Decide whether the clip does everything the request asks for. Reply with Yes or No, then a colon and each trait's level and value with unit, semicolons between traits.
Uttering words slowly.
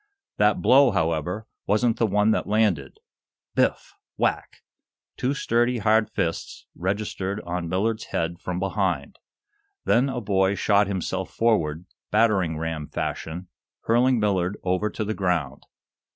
Yes: slow, 130 wpm